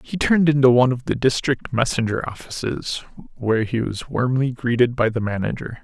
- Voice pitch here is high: No, low, 125 Hz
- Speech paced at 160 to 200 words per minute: Yes, average, 175 wpm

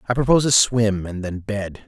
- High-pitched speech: No, low, 110 Hz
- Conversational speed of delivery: No, fast, 225 wpm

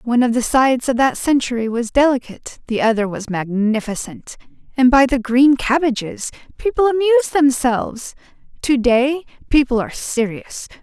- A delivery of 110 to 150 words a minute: Yes, average, 145 wpm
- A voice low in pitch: No, very high, 255 Hz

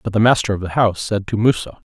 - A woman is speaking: No, male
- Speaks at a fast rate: Yes, fast, 285 wpm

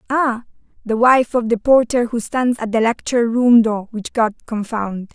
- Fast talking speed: No, average, 185 wpm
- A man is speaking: No, female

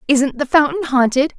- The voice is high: Yes, very high, 280 Hz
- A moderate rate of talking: Yes, average, 175 wpm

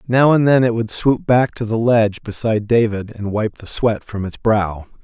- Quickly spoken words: Yes, fast, 225 wpm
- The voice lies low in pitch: Yes, low, 110 Hz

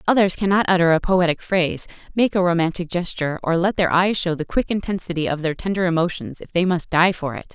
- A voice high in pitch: No, medium, 175 Hz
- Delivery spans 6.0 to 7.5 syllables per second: Yes, 6.2 syllables/s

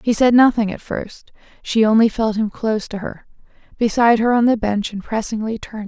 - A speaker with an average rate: No, fast, 215 wpm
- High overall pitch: Yes, high, 220 Hz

